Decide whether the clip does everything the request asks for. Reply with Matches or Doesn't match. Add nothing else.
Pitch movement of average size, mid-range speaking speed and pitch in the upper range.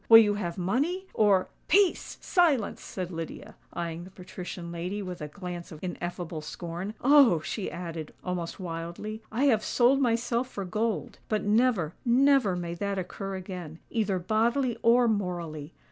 Matches